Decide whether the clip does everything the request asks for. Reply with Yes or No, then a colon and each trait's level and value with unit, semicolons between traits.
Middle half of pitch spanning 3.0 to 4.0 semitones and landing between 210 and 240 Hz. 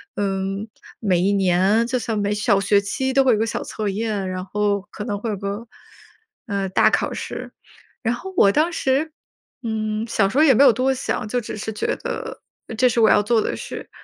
Yes: average, 3.3 semitones; high, 215 Hz